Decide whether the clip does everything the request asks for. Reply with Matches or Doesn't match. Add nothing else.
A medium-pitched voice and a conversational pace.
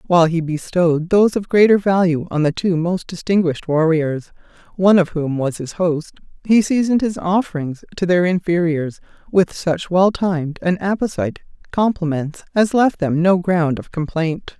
Matches